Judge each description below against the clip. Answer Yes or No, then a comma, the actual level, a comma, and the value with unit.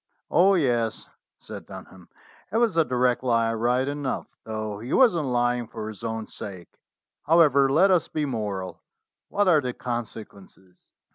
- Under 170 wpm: Yes, average, 155 wpm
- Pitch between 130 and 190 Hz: No, low, 120 Hz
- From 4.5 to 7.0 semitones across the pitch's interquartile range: Yes, average, 5.2 semitones